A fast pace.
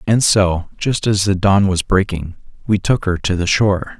Yes: fast, 210 wpm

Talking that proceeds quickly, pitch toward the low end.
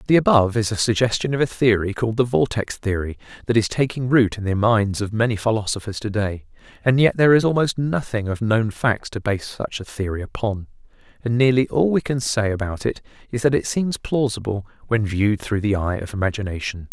Yes: fast, 210 wpm; low, 110 Hz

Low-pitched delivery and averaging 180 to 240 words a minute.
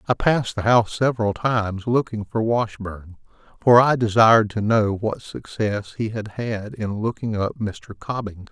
No: low, 110 Hz; average, 170 wpm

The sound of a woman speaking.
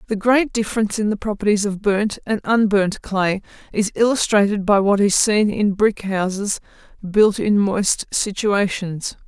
Yes: female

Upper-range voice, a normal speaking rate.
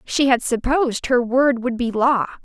Yes: very high, 250 Hz; average, 195 wpm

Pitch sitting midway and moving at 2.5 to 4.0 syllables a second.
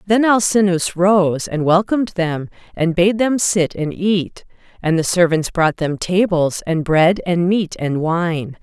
Yes: medium, 175 Hz; 3.8 syllables/s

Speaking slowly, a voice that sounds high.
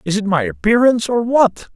No: fast, 205 wpm; high, 205 Hz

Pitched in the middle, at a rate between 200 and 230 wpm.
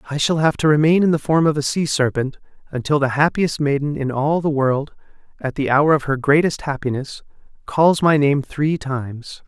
Yes: medium, 145 Hz; fast, 205 wpm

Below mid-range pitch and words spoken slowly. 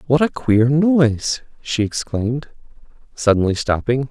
Yes: low, 130 Hz; slow, 115 wpm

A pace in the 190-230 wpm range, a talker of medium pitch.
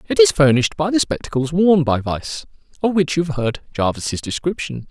Yes: average, 195 wpm; medium, 155 Hz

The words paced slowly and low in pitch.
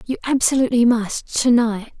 No: slow, 120 wpm; high, 240 Hz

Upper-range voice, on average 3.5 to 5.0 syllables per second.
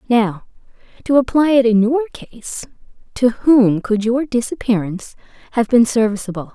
Yes: high, 235 Hz; 4.7 syllables/s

